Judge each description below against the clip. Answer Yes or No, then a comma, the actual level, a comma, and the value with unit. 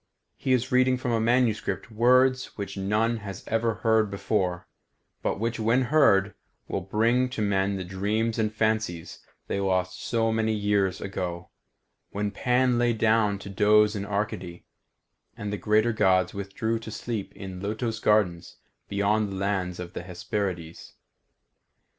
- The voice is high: No, low, 105 Hz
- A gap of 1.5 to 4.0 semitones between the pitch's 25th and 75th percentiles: Yes, average, 2.7 semitones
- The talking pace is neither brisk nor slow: Yes, average, 150 wpm